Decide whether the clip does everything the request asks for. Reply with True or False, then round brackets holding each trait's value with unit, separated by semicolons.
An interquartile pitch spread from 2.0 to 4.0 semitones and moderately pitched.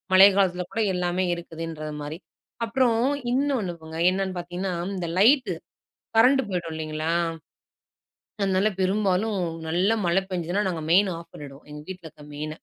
True (3.4 semitones; 180 Hz)